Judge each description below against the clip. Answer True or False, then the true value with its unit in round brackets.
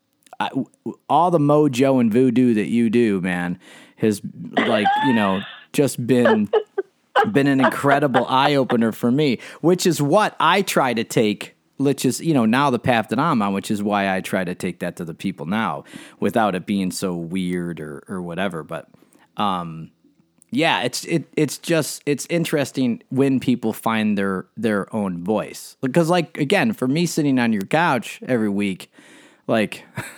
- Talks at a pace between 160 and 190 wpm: True (175 wpm)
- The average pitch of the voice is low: True (130 Hz)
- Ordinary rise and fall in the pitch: False (7.0 semitones)